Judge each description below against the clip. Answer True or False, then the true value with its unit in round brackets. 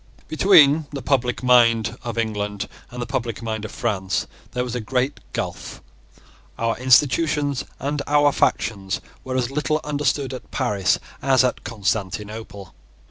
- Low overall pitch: True (125 Hz)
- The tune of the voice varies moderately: True (4.2 semitones)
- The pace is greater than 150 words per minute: False (140 wpm)